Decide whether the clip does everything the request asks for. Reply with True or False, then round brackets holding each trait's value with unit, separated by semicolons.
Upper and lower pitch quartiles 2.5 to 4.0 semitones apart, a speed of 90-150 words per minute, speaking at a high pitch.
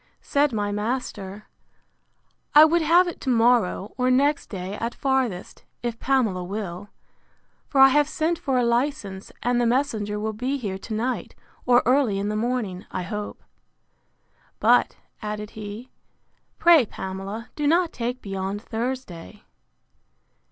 False (4.4 semitones; 145 wpm; 235 Hz)